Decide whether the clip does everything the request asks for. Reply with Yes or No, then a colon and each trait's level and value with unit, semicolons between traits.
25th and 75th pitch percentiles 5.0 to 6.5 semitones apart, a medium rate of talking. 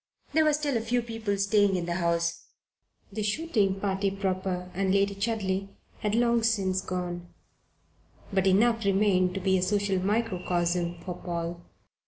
No: average, 2.8 semitones; average, 155 wpm